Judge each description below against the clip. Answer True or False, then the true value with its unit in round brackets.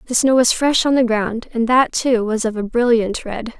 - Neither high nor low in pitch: False (235 Hz)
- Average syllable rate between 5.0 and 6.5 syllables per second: False (4.8 syllables/s)